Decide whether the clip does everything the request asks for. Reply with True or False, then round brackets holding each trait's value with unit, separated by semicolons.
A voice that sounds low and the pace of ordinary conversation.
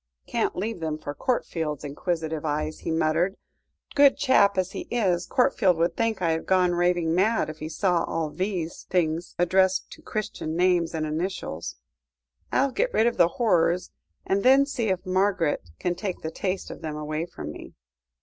False (175 Hz; 180 wpm)